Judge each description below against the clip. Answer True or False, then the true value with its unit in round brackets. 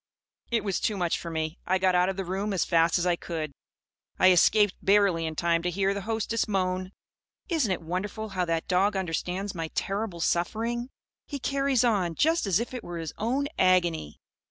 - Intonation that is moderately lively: True (3.8 semitones)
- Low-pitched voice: False (190 Hz)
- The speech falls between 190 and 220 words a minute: True (200 wpm)